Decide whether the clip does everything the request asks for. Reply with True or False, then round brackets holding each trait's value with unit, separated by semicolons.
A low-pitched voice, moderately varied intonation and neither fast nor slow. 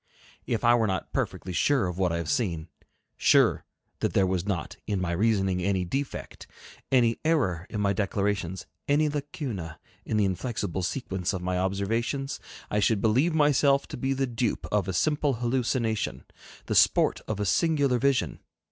False (105 Hz; 6.0 semitones; 170 wpm)